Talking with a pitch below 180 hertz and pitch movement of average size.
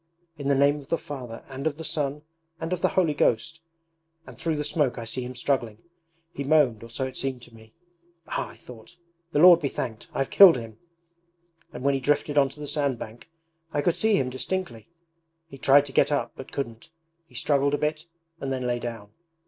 Yes: medium, 140 Hz; average, 3.4 semitones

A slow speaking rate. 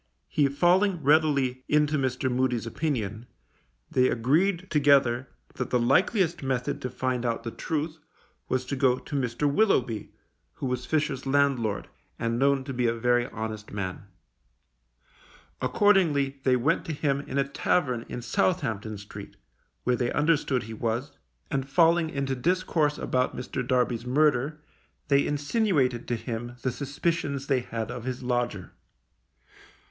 No: average, 145 wpm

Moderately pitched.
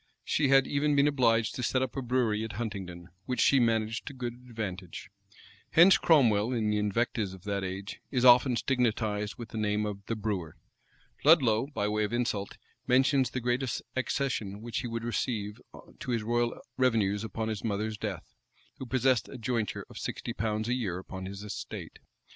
No: low, 115 Hz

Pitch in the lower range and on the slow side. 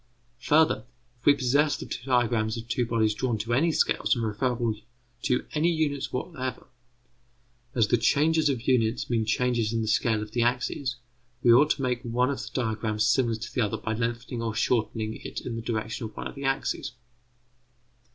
No: low, 120 Hz; average, 190 wpm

